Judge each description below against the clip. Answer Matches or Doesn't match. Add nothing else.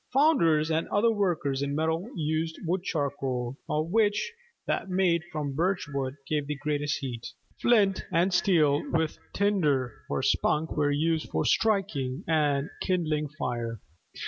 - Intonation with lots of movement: Doesn't match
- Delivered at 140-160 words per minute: Matches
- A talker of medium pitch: Matches